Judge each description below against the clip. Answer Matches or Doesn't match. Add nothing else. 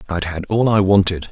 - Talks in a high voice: Doesn't match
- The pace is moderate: Doesn't match